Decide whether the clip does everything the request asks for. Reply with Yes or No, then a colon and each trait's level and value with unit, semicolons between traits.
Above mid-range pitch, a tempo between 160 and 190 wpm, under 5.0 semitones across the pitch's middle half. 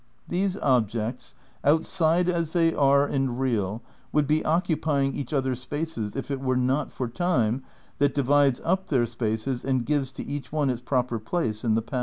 No: low, 135 Hz; average, 180 wpm; average, 3.9 semitones